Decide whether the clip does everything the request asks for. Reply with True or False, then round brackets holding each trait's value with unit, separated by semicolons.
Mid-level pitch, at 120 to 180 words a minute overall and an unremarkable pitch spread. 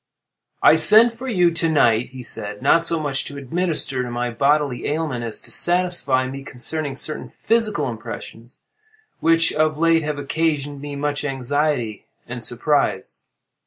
True (145 Hz; 155 wpm; 4.4 semitones)